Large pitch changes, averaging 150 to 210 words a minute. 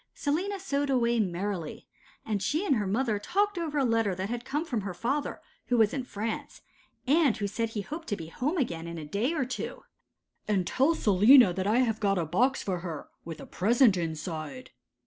Yes: wide, 6.3 semitones; fast, 205 wpm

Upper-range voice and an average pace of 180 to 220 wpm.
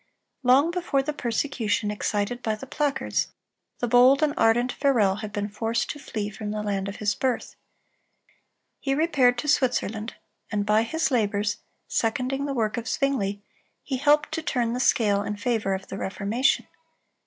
No: high, 235 Hz; average, 165 wpm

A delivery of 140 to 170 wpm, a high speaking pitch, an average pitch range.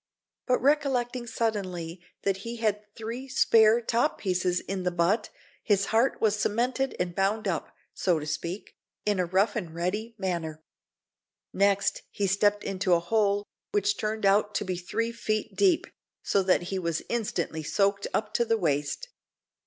Yes: average, 160 wpm; high, 205 Hz; average, 3.7 semitones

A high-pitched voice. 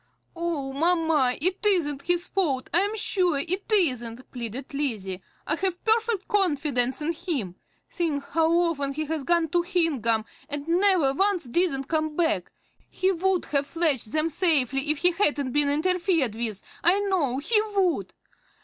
Yes: very high, 320 Hz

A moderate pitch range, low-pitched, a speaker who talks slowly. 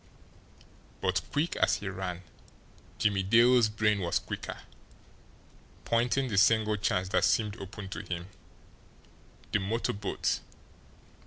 Yes: average, 3.1 semitones; low, 105 Hz; slow, 115 wpm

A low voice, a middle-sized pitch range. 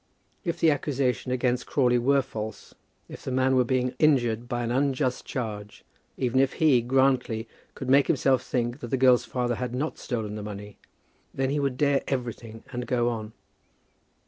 No: low, 125 Hz; narrow, 2.0 semitones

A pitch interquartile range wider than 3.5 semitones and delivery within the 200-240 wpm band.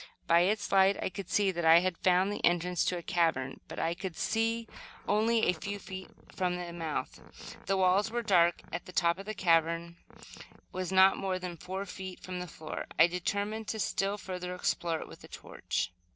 No: narrow, 2.4 semitones; fast, 205 wpm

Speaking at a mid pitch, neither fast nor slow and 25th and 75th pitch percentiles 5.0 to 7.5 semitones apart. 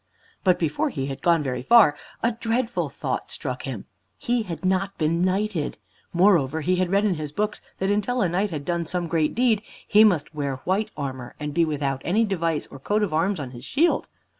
No: medium, 175 Hz; fast, 210 wpm; wide, 5.6 semitones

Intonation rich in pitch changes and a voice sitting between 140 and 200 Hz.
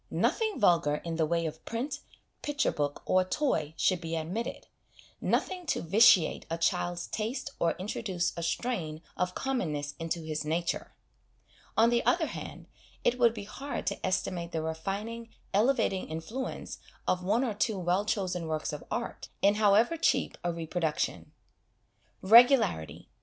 Yes: wide, 6.0 semitones; medium, 185 Hz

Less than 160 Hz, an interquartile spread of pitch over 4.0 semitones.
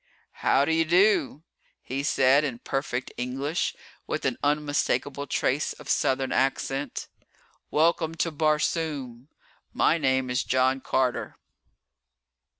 No: medium, 140 Hz; average, 2.7 semitones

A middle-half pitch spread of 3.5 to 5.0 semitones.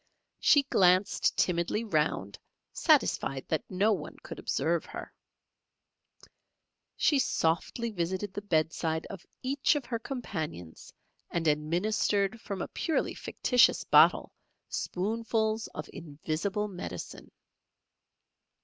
No: wide, 5.4 semitones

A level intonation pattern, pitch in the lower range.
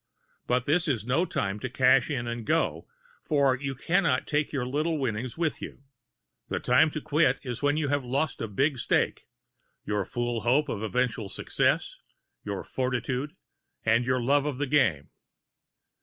No: average, 3.4 semitones; low, 130 Hz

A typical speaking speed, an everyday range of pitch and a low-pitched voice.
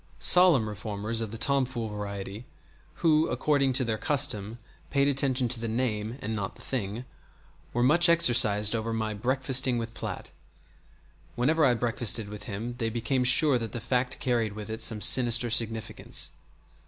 Yes: average, 165 wpm; average, 3.2 semitones; low, 115 Hz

